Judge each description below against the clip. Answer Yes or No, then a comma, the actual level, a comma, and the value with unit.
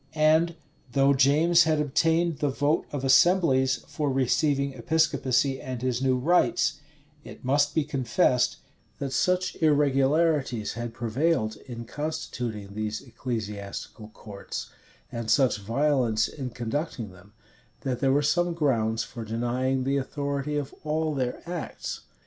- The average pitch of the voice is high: No, low, 135 Hz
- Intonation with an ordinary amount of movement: Yes, average, 4.1 semitones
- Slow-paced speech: Yes, slow, 130 wpm